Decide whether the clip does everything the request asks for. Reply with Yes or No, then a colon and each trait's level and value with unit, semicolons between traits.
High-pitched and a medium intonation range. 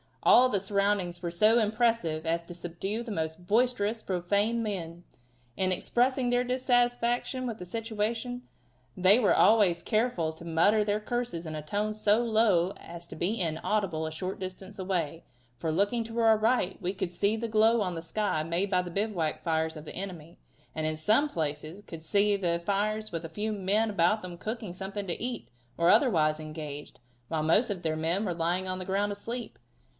Yes: high, 195 Hz; average, 4.5 semitones